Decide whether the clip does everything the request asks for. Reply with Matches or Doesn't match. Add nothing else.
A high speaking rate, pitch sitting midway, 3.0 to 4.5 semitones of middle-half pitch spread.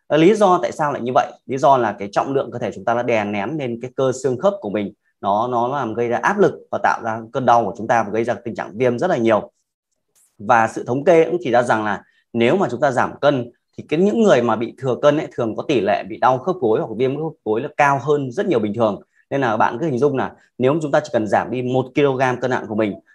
Doesn't match